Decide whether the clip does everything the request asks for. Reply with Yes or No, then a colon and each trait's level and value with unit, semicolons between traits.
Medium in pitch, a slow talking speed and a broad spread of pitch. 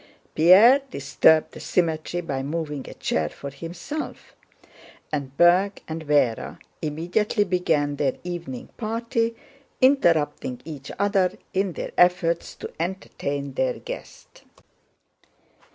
No: medium, 165 Hz; slow, 110 wpm; average, 4.7 semitones